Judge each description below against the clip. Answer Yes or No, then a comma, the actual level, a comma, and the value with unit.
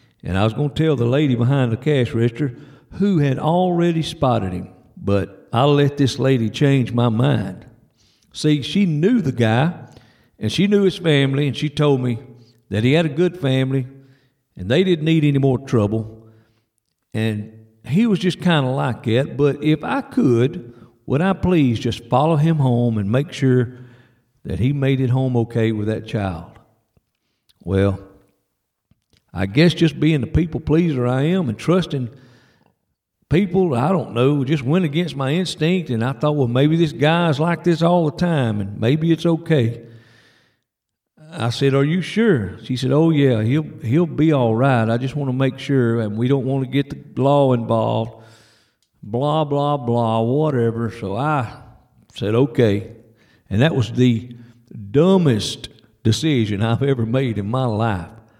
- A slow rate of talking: No, average, 175 wpm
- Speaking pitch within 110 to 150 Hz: Yes, low, 130 Hz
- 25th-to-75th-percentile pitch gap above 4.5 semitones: Yes, average, 4.9 semitones